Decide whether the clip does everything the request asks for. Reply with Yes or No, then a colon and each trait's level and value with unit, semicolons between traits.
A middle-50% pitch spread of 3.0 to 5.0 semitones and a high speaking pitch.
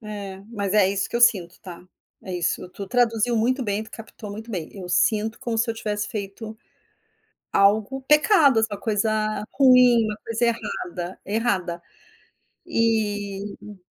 No: narrow, 2.5 semitones; high, 215 Hz